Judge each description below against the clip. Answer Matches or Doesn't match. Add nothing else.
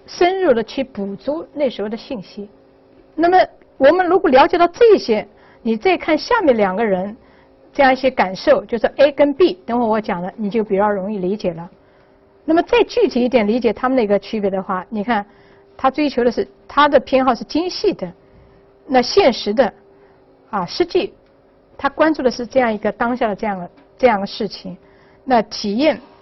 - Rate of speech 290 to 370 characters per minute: Doesn't match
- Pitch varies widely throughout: Matches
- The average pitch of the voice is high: Matches